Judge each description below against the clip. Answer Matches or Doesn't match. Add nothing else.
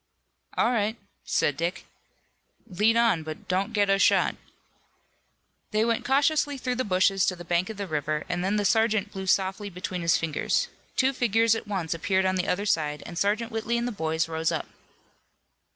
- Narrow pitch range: Doesn't match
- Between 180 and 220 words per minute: Matches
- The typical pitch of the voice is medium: Doesn't match